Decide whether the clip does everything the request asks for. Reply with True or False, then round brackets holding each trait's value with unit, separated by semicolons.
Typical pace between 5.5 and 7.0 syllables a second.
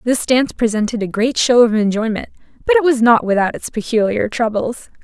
True (5.6 syllables/s)